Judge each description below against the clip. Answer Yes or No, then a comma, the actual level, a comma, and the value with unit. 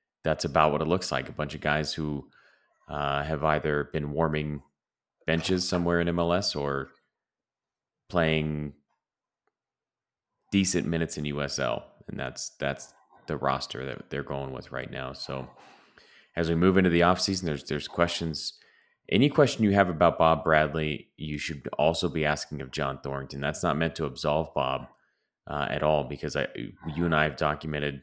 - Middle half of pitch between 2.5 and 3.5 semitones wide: Yes, average, 2.8 semitones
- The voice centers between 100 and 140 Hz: No, very low, 75 Hz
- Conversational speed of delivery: Yes, average, 165 wpm